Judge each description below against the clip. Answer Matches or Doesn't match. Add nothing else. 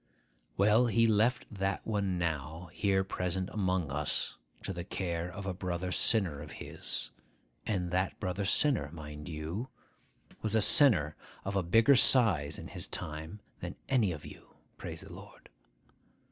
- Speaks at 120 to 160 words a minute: Matches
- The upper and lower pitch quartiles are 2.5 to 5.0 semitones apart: Matches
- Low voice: Matches